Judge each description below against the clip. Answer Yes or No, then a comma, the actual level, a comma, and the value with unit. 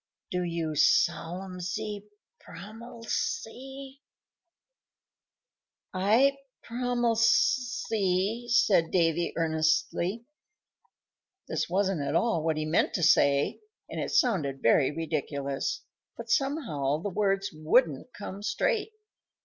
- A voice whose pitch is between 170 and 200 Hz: Yes, medium, 185 Hz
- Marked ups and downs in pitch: Yes, wide, 6.3 semitones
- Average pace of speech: No, slow, 95 wpm